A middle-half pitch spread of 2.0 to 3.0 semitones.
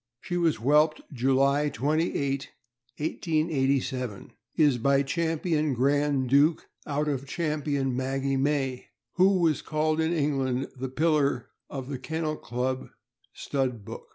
Yes: average, 2.7 semitones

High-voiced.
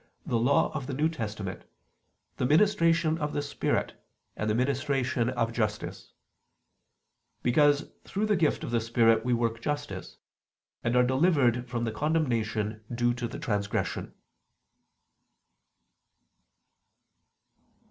No: low, 125 Hz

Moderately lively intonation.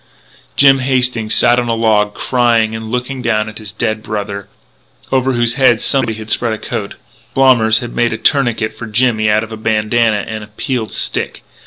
No: narrow, 2.3 semitones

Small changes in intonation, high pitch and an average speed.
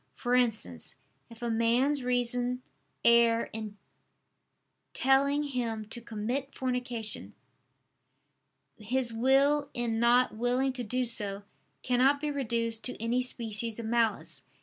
No: narrow, 2.0 semitones; high, 240 Hz; slow, 120 wpm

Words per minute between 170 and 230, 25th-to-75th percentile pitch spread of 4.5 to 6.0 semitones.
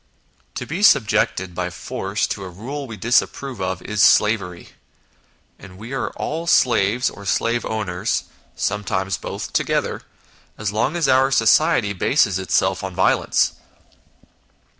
No: slow, 135 wpm; average, 5.3 semitones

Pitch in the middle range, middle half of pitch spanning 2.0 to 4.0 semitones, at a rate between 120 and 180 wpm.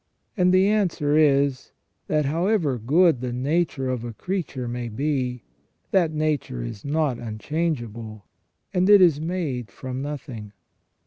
No: medium, 145 Hz; average, 5.3 semitones; slow, 135 wpm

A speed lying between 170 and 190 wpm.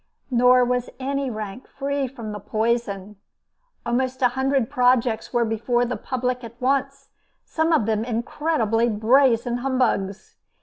No: slow, 135 wpm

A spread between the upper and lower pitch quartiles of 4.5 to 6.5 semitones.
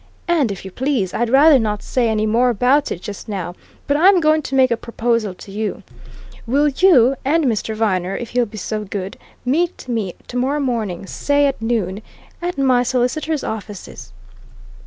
Yes: average, 4.9 semitones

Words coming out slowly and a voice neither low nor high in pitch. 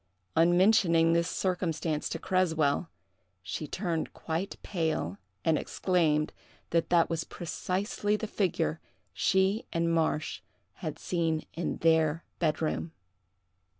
Yes: slow, 115 wpm; medium, 165 Hz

